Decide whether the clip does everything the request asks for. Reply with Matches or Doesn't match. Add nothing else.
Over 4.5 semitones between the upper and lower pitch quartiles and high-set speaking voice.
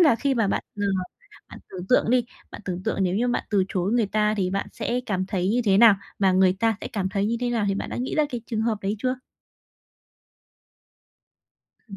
Doesn't match